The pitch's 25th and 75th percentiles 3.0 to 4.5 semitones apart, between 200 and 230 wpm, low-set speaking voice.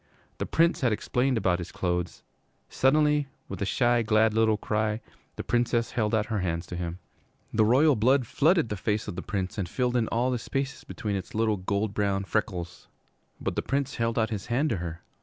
Yes: average, 4.1 semitones; fast, 205 wpm; low, 110 Hz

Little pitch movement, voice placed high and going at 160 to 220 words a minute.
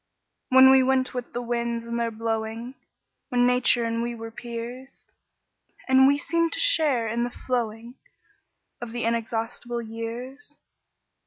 No: narrow, 2.1 semitones; high, 240 Hz; average, 145 wpm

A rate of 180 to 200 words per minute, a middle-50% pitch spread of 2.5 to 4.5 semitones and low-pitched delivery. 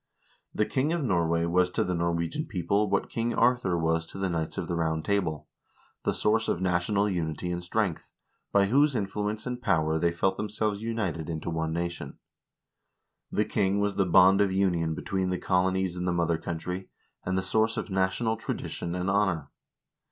Yes: average, 190 wpm; average, 3.4 semitones; very low, 95 Hz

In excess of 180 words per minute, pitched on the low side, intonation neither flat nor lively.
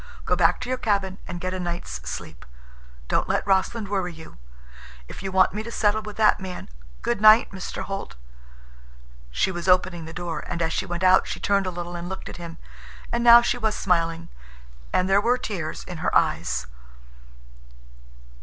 No: average, 190 wpm; medium, 185 Hz; average, 3.2 semitones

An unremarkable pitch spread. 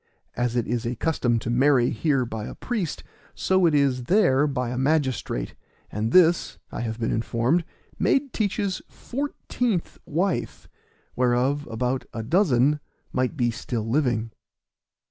No: wide, 5.7 semitones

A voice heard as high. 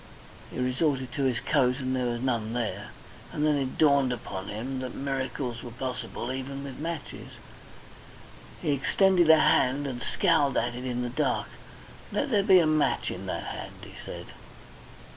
No: low, 130 Hz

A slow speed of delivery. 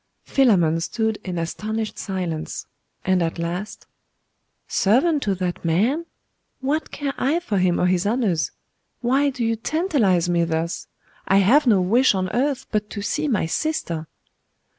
No: average, 150 wpm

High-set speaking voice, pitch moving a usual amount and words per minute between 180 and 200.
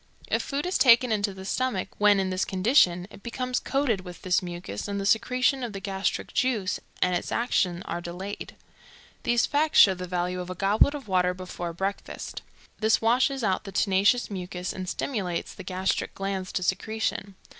Yes: high, 195 Hz; average, 4.2 semitones; average, 185 wpm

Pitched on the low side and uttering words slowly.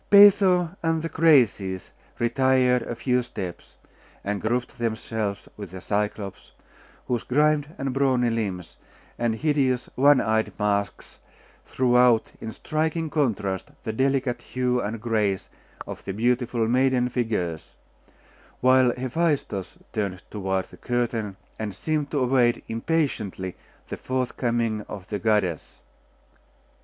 Yes: low, 120 Hz; slow, 125 wpm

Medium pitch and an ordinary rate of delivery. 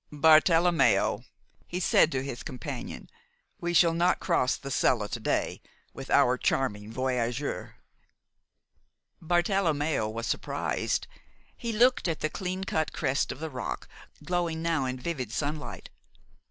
No: medium, 155 Hz; slow, 130 wpm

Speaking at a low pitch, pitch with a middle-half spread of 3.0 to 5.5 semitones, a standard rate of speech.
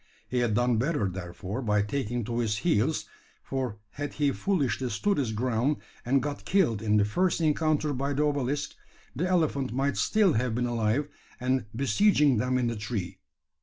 Yes: low, 125 Hz; average, 4.6 semitones; average, 175 wpm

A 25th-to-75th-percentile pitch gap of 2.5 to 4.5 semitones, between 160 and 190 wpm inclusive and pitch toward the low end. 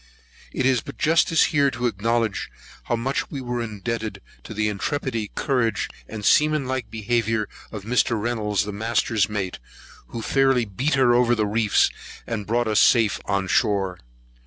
Yes: average, 3.0 semitones; average, 165 wpm; low, 115 Hz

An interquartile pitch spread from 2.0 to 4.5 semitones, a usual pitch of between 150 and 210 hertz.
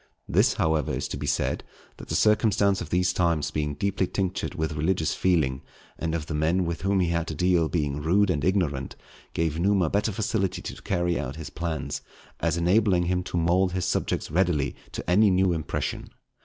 No: average, 3.0 semitones; very low, 85 Hz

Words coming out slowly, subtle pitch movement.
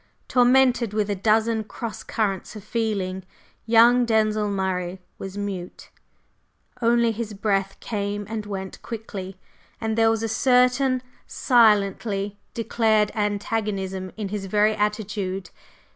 Yes: slow, 120 wpm; narrow, 2.3 semitones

